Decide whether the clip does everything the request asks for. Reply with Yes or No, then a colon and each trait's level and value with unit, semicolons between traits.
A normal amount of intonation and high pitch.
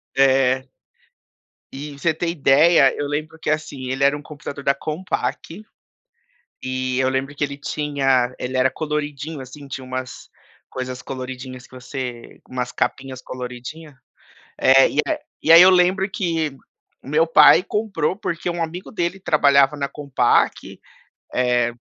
No: average, 3.4 semitones; medium, 140 Hz